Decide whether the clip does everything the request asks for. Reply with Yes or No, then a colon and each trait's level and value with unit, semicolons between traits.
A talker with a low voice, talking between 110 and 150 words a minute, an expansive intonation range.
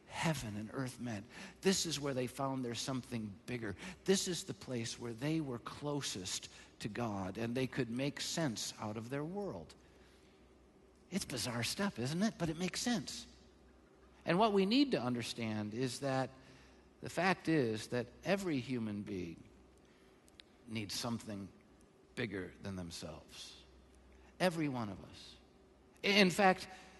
Yes: low, 125 Hz; average, 145 wpm; wide, 7.1 semitones